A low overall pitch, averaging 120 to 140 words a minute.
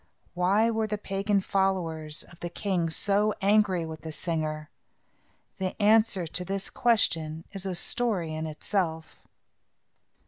No: medium, 185 Hz; slow, 135 wpm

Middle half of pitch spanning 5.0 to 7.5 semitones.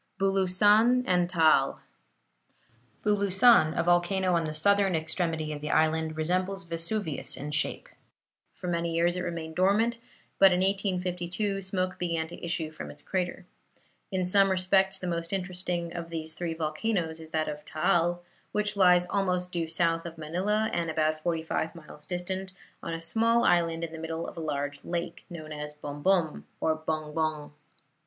No: average, 2.8 semitones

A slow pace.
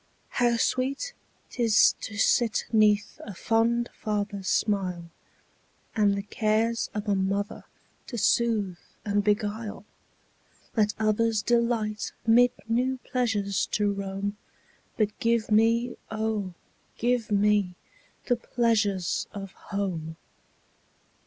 Yes: slow, 100 wpm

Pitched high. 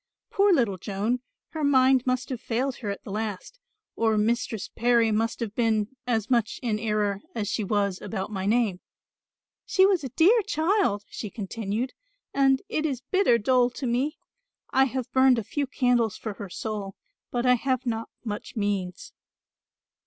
Yes: high, 235 Hz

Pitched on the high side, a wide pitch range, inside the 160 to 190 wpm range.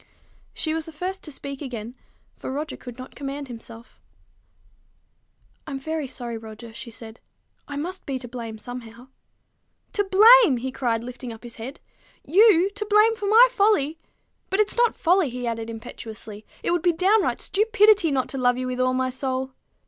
Yes: very high, 270 Hz; wide, 7.4 semitones; average, 180 wpm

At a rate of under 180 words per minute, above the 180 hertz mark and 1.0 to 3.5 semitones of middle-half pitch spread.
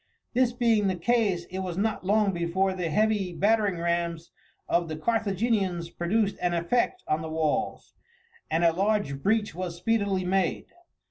No: average, 155 wpm; high, 190 Hz; average, 4.0 semitones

